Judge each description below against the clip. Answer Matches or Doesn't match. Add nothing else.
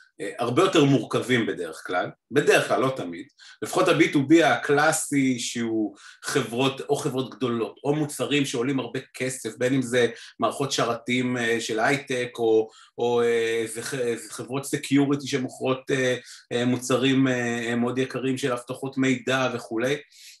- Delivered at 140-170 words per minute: Doesn't match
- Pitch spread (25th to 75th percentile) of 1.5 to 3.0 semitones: Matches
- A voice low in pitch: Matches